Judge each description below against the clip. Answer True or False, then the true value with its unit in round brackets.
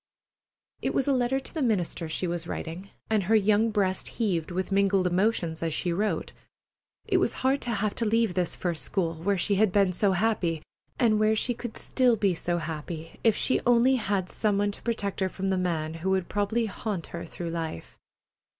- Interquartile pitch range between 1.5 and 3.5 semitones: False (4.0 semitones)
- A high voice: True (195 Hz)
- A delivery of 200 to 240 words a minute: True (205 wpm)